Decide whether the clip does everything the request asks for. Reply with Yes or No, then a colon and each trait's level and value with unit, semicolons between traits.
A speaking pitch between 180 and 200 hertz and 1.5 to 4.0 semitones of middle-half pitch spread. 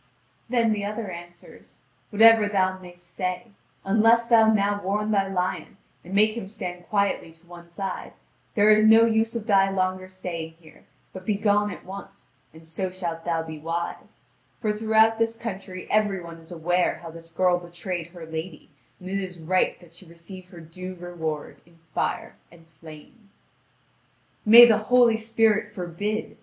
Yes: medium, 185 Hz; average, 3.7 semitones